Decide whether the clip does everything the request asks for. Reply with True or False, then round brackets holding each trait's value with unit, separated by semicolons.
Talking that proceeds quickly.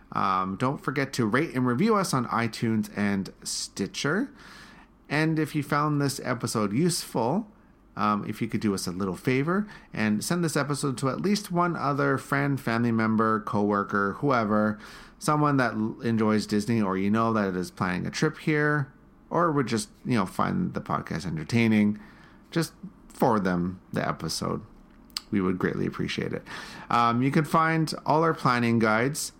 False (170 wpm)